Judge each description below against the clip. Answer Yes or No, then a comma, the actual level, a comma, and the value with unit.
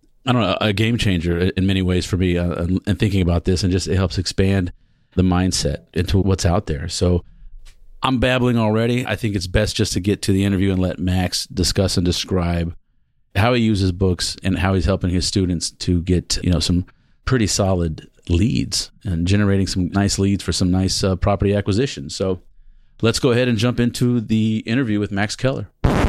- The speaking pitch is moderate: No, very low, 95 Hz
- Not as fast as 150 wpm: No, average, 200 wpm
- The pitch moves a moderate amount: Yes, average, 3.2 semitones